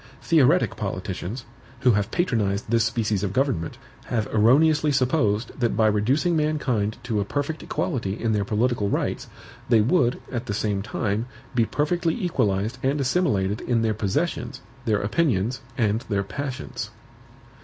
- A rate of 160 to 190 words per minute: No, average, 145 wpm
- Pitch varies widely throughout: No, average, 5.0 semitones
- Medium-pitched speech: No, low, 115 Hz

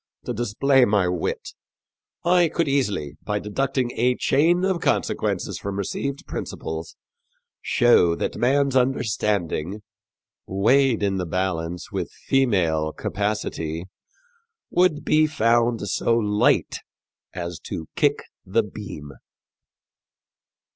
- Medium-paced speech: No, slow, 105 wpm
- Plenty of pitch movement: Yes, wide, 6.8 semitones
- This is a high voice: No, low, 105 Hz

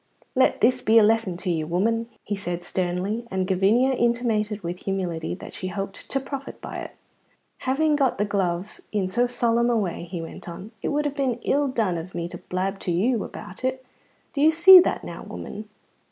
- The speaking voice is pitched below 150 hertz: No, high, 210 Hz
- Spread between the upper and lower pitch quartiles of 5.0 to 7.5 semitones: Yes, average, 5.3 semitones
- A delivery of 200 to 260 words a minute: Yes, fast, 205 wpm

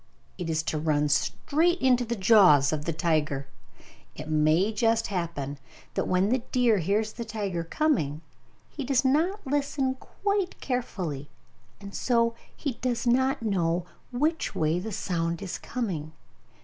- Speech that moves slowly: No, average, 150 wpm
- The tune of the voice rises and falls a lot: Yes, wide, 7.7 semitones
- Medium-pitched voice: No, high, 205 Hz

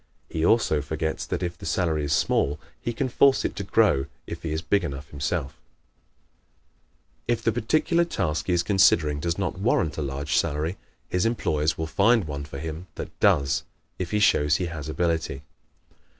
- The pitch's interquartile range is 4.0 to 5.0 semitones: Yes, average, 4.4 semitones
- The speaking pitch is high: No, very low, 80 Hz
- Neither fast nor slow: Yes, average, 180 wpm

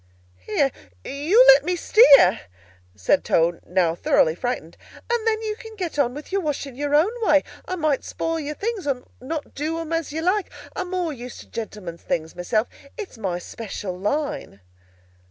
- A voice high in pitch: Yes, very high, 290 Hz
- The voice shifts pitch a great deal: Yes, wide, 9.0 semitones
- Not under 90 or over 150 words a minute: No, average, 175 wpm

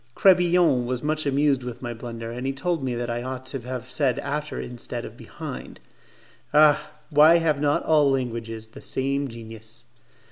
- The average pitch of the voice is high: No, low, 130 Hz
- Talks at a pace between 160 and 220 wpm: Yes, average, 175 wpm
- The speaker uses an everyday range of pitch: Yes, average, 3.7 semitones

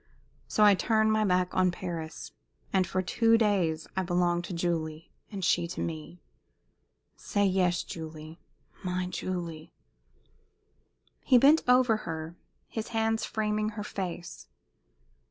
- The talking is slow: Yes, slow, 130 wpm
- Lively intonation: No, average, 4.0 semitones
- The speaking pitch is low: No, medium, 185 Hz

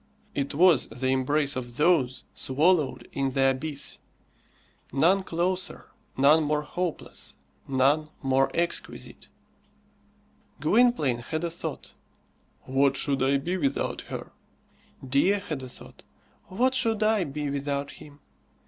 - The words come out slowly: Yes, slow, 120 wpm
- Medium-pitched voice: Yes, medium, 145 Hz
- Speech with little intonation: No, average, 4.4 semitones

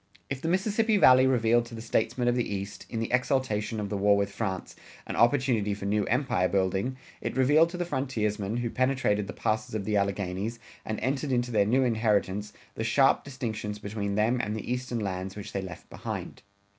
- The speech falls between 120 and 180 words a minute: No, average, 200 wpm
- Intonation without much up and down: No, average, 3.9 semitones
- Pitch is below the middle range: Yes, low, 110 Hz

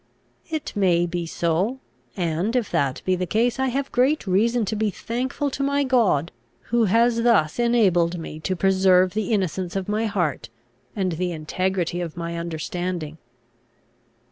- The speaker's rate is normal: Yes, average, 160 wpm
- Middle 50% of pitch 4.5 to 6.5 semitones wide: Yes, average, 5.2 semitones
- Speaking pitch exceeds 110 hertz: Yes, high, 190 Hz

